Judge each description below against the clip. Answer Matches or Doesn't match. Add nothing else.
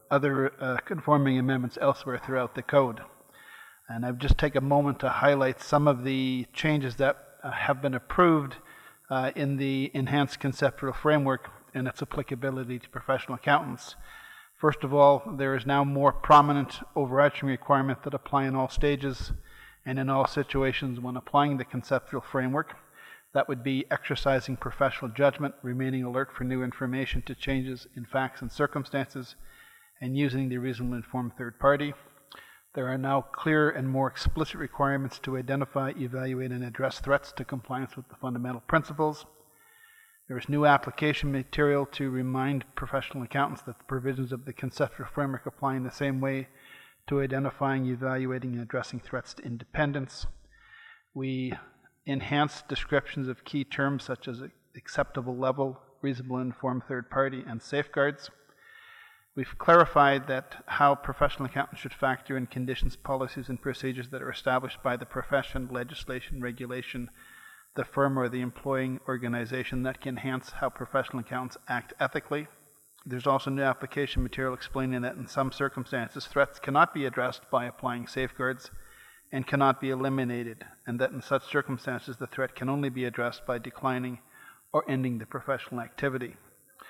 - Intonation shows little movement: Matches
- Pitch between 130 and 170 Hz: Matches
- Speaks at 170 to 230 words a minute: Doesn't match